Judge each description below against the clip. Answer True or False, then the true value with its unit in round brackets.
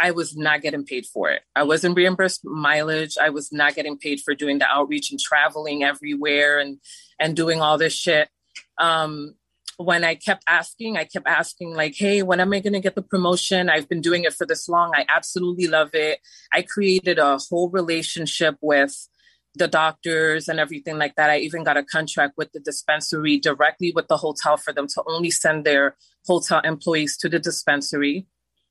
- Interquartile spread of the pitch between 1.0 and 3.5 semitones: True (2.8 semitones)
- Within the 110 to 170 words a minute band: False (195 wpm)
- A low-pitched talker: False (155 Hz)